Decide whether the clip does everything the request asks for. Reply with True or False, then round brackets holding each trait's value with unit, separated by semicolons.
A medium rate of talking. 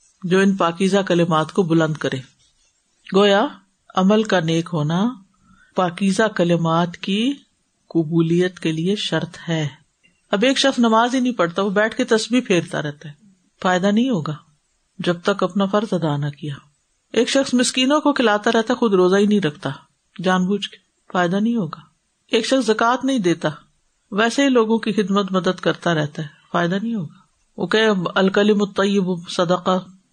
True (165 wpm)